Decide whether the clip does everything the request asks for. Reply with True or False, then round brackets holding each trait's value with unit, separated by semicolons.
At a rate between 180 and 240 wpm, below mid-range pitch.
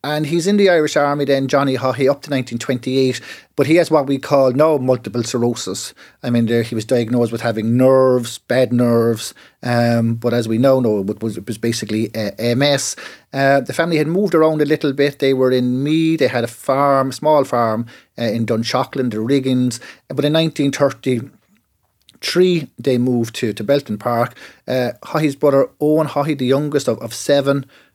True (190 wpm; 130 Hz)